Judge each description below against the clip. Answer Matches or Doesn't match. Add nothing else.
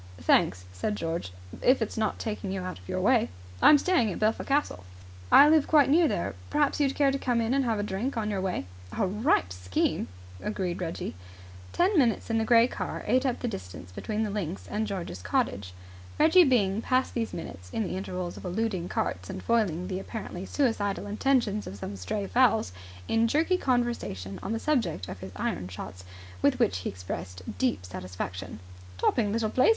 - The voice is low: Doesn't match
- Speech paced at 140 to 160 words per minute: Doesn't match